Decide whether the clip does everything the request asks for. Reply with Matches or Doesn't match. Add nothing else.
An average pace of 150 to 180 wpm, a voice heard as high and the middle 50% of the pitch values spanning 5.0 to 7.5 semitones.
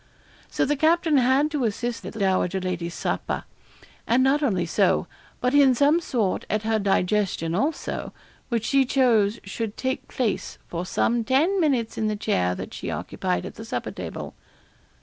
Matches